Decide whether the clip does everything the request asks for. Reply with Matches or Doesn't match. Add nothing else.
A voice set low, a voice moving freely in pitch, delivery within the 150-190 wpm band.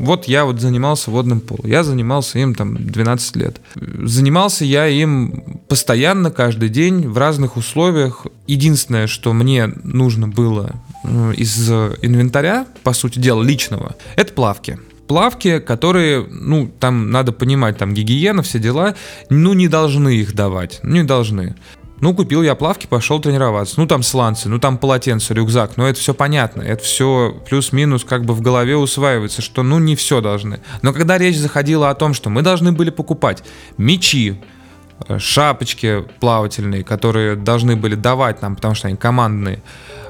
Doesn't match